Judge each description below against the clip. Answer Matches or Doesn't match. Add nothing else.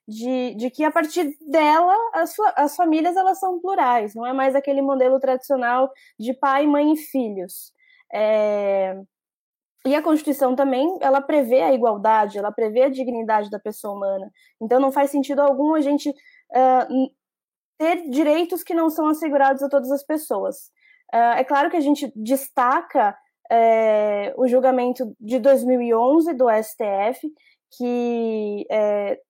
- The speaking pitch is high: Matches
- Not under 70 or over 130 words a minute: Doesn't match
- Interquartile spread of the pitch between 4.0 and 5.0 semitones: Matches